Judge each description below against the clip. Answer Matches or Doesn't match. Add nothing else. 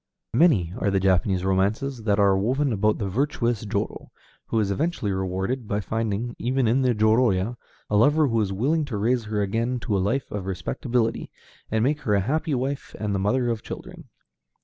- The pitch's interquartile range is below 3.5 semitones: Doesn't match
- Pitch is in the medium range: Doesn't match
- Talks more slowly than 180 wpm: Doesn't match